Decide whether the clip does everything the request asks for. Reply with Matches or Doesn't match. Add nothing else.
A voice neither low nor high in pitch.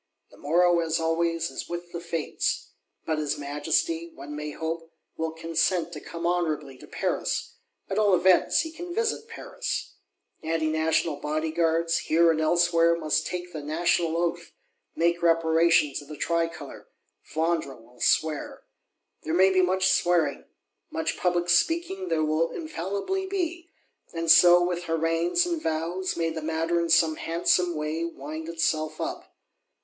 Matches